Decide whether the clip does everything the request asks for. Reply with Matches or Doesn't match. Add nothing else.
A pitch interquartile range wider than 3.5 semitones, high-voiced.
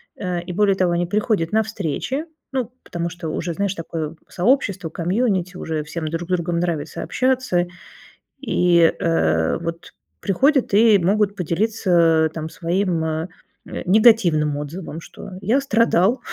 Doesn't match